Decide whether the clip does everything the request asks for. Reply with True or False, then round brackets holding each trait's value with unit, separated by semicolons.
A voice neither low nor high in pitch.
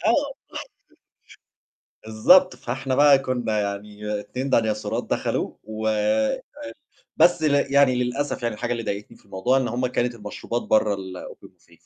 False (115 Hz)